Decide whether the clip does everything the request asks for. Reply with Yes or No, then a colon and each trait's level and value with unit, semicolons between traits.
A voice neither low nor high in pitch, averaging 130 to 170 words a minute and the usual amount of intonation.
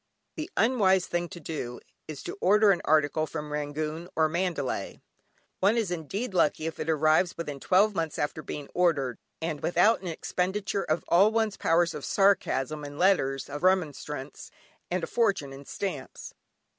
Yes: medium, 165 Hz; average, 165 wpm; average, 4.2 semitones